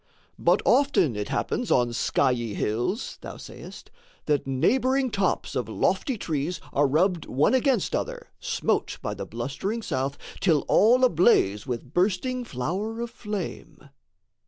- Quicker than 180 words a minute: No, slow, 135 wpm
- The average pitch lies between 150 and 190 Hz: Yes, medium, 185 Hz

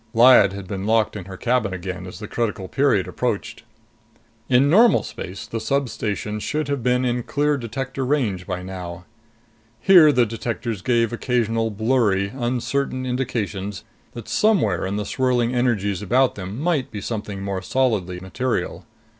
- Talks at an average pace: Yes, average, 155 wpm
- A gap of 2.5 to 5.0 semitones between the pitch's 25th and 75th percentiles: Yes, average, 4.5 semitones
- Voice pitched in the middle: No, low, 115 Hz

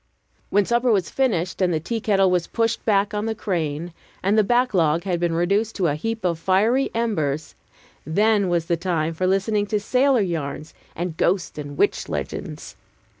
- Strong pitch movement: No, average, 4.6 semitones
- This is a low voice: No, high, 190 Hz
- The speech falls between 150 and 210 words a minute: Yes, average, 180 wpm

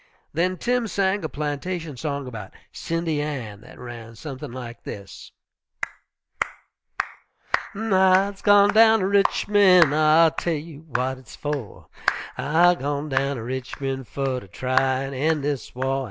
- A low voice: No, medium, 145 Hz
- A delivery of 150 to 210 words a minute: No, average, 140 wpm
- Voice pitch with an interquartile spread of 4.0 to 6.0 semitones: Yes, average, 5.3 semitones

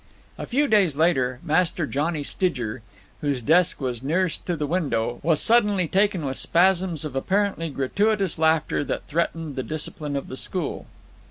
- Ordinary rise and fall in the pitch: Yes, average, 4.7 semitones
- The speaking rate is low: No, average, 160 wpm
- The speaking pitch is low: No, medium, 160 Hz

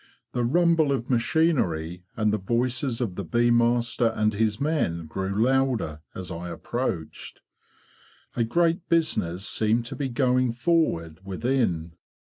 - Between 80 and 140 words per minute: Yes, slow, 135 wpm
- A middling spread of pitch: No, wide, 5.7 semitones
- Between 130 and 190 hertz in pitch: No, low, 120 Hz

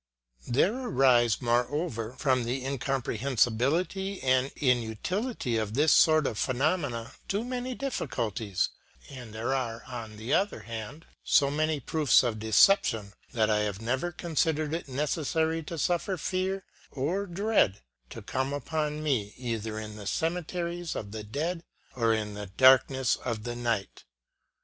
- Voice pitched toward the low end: Yes, low, 130 Hz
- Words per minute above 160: No, average, 145 wpm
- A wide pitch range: Yes, wide, 6.1 semitones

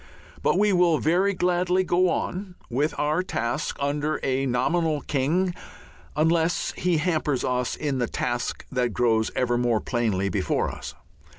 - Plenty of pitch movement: Yes, wide, 6.1 semitones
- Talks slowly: No, average, 150 wpm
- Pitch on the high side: No, medium, 150 Hz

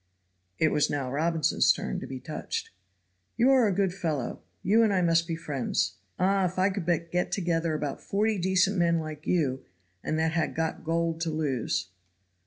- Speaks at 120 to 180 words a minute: No, average, 190 wpm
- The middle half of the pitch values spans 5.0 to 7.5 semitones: No, average, 3.3 semitones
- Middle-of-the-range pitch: Yes, medium, 165 Hz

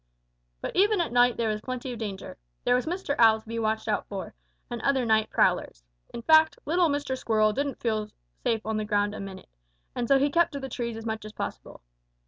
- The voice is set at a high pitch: Yes, high, 235 Hz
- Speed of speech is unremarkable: No, fast, 225 wpm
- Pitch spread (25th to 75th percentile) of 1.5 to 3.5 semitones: No, average, 4.3 semitones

